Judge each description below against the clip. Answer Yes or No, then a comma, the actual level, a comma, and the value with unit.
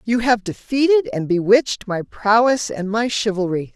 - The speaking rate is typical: Yes, average, 160 wpm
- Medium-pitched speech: No, high, 225 Hz